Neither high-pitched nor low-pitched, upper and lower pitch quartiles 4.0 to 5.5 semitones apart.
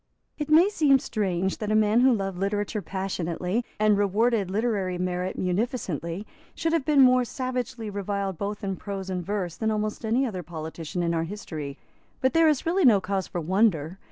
No: high, 205 Hz; average, 4.6 semitones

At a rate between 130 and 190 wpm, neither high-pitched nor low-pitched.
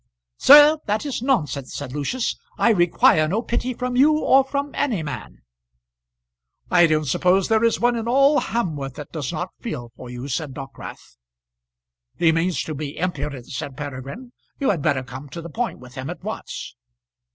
Yes: average, 175 wpm; medium, 170 Hz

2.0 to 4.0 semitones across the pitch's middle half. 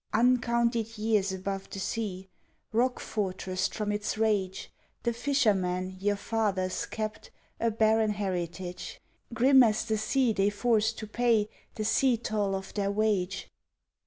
Yes: average, 2.7 semitones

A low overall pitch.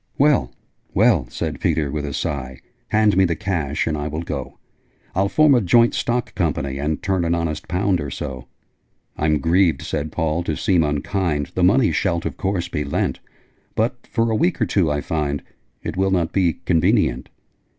Yes: very low, 85 Hz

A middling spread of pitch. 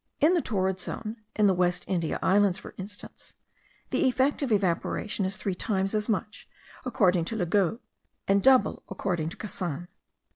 Yes: average, 3.3 semitones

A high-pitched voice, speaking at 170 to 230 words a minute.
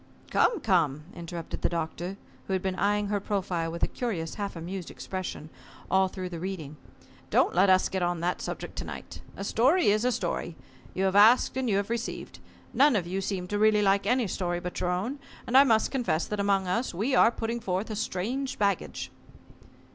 Yes: high, 195 Hz; fast, 205 wpm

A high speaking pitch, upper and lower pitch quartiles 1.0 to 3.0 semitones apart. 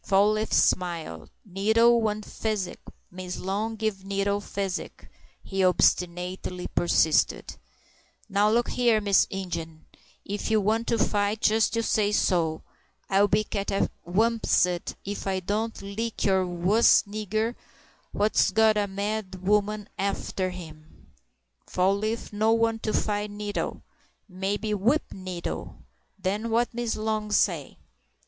Yes: high, 205 Hz; average, 2.7 semitones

